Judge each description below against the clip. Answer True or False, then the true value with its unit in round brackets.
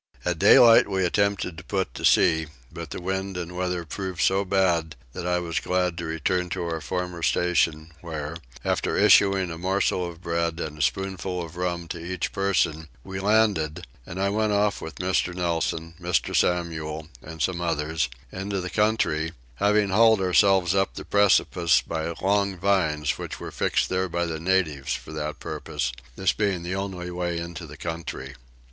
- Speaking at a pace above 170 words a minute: True (180 wpm)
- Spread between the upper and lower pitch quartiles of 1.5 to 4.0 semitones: True (2.8 semitones)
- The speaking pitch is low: True (90 Hz)